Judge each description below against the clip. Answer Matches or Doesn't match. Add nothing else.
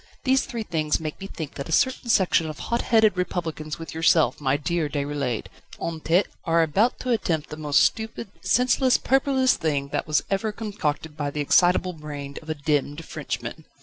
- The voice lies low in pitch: Doesn't match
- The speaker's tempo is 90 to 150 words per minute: Doesn't match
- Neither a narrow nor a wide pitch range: Doesn't match